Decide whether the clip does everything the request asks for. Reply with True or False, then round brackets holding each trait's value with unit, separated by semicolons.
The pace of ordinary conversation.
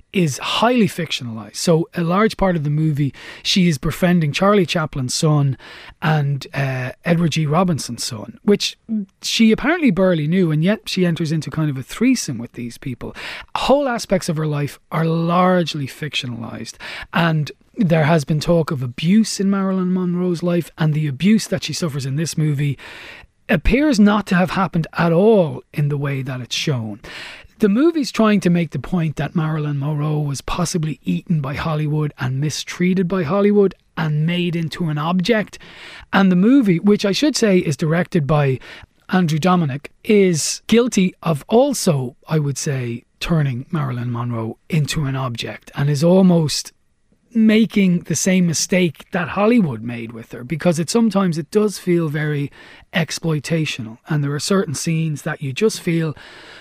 True (165 wpm)